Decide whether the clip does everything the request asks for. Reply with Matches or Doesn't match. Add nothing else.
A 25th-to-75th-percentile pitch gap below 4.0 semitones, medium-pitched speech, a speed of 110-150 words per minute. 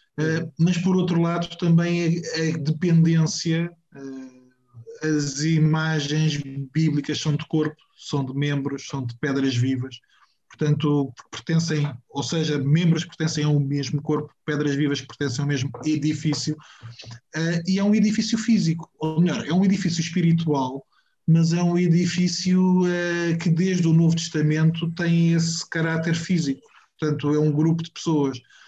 Matches